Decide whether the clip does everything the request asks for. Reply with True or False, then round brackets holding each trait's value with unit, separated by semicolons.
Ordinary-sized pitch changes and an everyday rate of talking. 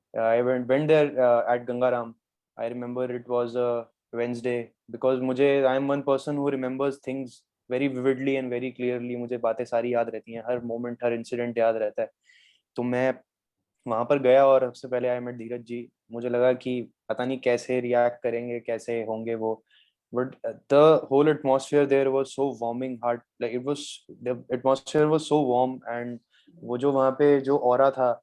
False (1.9 semitones; 195 wpm)